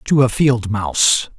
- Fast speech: No, average, 175 wpm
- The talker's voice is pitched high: No, low, 120 Hz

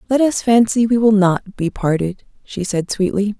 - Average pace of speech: Yes, average, 195 wpm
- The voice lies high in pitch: Yes, high, 205 Hz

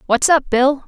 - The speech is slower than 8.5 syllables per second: Yes, 4.6 syllables/s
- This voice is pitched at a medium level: No, very high, 270 Hz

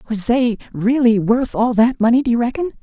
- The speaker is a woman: No, male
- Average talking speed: No, fast, 210 wpm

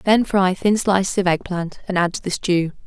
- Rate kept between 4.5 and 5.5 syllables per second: Yes, 5.0 syllables/s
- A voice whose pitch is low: No, medium, 185 Hz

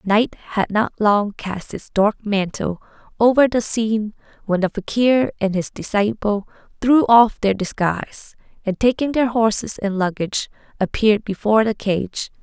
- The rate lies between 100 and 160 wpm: Yes, average, 150 wpm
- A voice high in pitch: Yes, high, 210 Hz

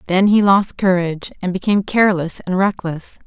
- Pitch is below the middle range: No, medium, 185 Hz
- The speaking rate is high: No, average, 165 wpm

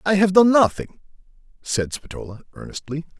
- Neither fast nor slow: No, slow, 130 wpm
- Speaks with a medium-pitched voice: Yes, medium, 170 Hz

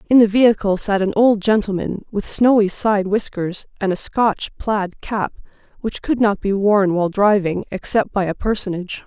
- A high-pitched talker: Yes, high, 205 Hz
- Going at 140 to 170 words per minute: No, average, 180 wpm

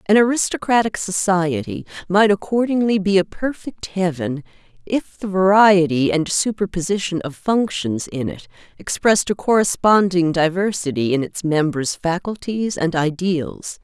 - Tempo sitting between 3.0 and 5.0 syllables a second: Yes, 4.6 syllables/s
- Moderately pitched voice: Yes, medium, 180 Hz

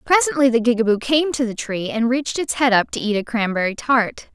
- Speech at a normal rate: No, fast, 235 wpm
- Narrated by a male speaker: No, female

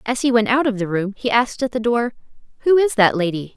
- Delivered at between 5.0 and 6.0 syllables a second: No, 6.2 syllables/s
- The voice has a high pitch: Yes, high, 230 Hz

